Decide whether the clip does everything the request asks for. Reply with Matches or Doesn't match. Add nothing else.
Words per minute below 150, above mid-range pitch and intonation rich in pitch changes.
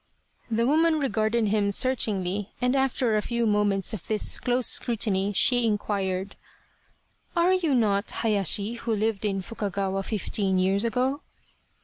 Doesn't match